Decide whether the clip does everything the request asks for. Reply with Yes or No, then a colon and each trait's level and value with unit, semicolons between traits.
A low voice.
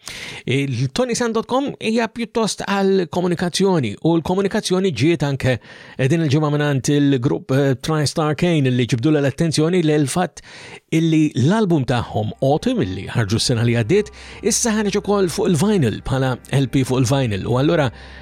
No: medium, 155 Hz